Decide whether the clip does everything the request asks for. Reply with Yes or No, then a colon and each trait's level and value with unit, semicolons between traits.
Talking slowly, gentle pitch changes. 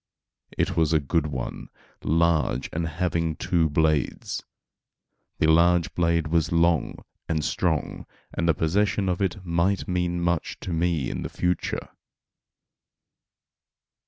Yes: slow, 130 wpm; narrow, 1.7 semitones